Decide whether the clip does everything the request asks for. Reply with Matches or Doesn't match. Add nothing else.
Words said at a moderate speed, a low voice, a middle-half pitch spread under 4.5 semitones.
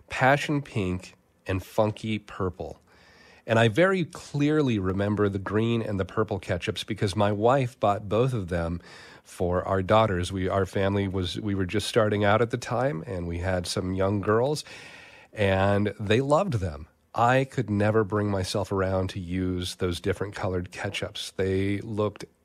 Matches